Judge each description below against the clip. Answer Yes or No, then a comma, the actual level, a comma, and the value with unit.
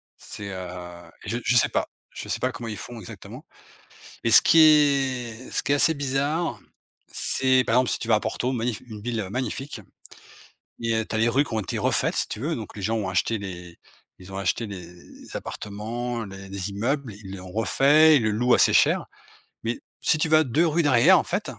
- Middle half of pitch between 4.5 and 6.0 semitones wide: Yes, average, 4.8 semitones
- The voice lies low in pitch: Yes, low, 115 Hz